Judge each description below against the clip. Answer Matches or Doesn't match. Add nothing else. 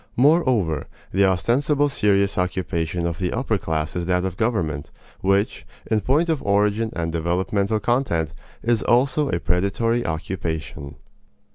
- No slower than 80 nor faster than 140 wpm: Matches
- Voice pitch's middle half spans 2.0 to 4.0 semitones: Doesn't match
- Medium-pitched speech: Doesn't match